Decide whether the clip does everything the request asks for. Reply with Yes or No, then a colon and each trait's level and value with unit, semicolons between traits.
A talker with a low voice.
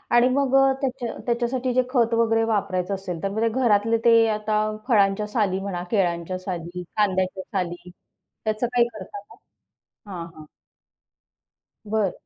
No: high, 210 Hz